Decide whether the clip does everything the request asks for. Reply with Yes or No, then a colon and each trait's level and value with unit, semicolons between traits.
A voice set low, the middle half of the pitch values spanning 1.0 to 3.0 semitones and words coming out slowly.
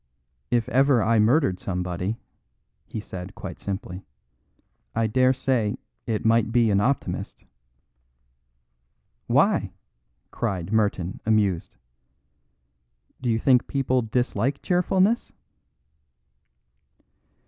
No: low, 110 Hz; average, 4.5 semitones; slow, 95 wpm